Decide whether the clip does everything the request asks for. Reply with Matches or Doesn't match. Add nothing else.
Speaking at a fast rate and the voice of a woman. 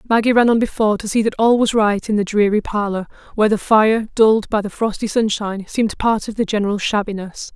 Matches